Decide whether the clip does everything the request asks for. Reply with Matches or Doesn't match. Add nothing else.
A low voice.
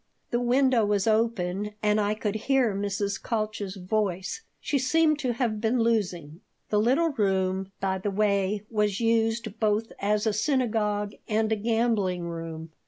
Doesn't match